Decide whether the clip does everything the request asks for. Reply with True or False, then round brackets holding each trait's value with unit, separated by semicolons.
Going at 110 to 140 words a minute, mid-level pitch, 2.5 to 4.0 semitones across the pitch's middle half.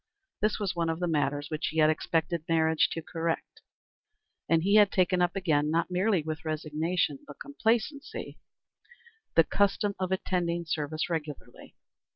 False (155 wpm; 165 Hz; 3.0 semitones)